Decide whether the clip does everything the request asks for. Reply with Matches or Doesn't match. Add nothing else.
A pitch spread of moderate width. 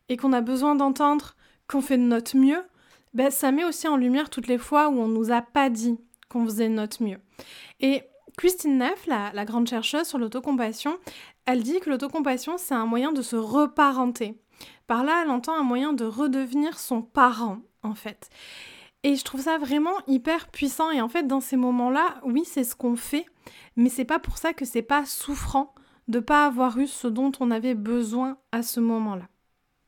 Matches